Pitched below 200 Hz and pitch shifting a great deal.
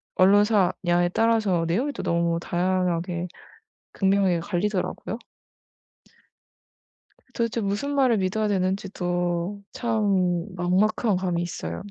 No: medium, 185 Hz; average, 3.0 semitones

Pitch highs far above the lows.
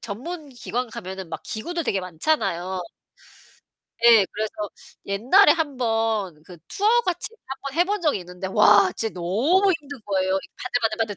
Yes: wide, 7.1 semitones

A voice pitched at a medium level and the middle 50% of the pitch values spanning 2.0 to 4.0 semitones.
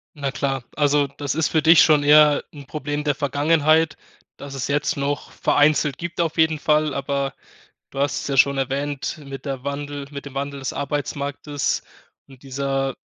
No: medium, 145 Hz; narrow, 1.4 semitones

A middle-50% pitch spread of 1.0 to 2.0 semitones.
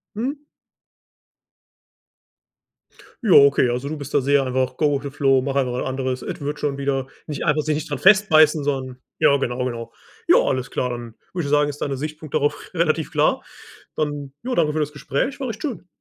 No: average, 2.7 semitones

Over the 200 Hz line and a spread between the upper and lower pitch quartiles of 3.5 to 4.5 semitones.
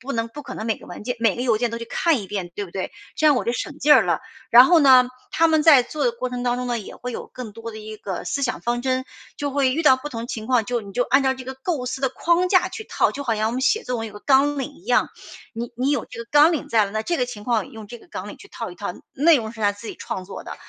Yes: very high, 250 Hz; average, 4.0 semitones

